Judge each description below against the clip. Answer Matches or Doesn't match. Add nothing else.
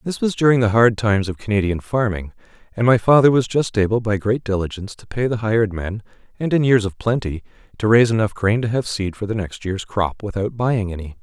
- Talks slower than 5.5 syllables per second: Doesn't match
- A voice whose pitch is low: Matches